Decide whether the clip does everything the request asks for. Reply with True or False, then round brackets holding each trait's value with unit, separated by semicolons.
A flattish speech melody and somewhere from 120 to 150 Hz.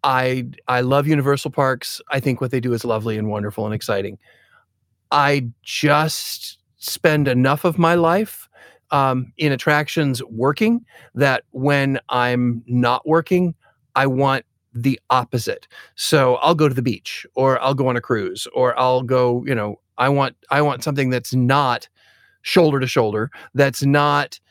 False (3.0 semitones; 135 Hz)